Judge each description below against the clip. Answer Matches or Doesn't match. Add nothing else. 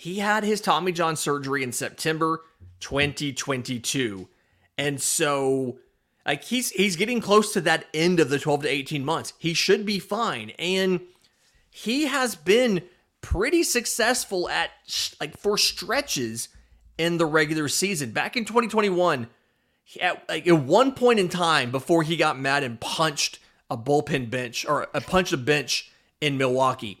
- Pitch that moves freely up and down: Matches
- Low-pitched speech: Doesn't match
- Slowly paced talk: Doesn't match